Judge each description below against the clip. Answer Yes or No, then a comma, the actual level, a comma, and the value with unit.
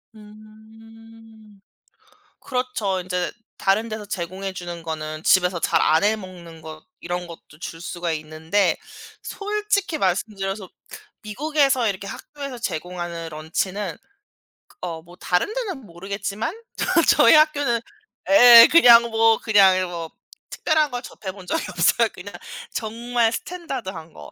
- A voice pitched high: Yes, high, 205 Hz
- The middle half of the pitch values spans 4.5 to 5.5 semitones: Yes, average, 5.1 semitones